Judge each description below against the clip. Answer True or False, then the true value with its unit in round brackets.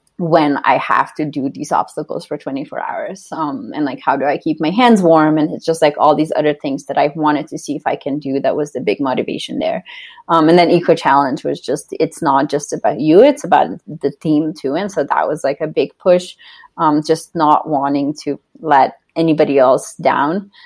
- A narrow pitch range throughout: False (3.8 semitones)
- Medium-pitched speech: True (155 Hz)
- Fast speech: True (225 wpm)